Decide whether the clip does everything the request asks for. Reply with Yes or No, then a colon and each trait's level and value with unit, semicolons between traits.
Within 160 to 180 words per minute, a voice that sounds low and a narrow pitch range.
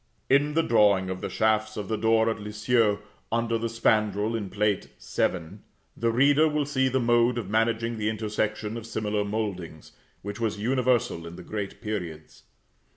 Yes: average, 170 wpm; low, 110 Hz; narrow, 2.1 semitones